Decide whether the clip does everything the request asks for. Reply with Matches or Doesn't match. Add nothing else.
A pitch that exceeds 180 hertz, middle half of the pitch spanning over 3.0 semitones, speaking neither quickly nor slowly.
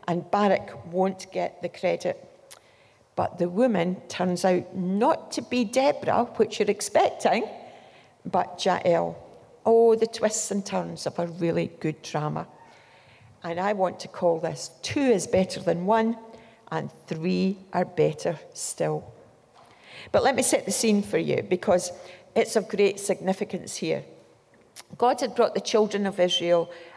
Matches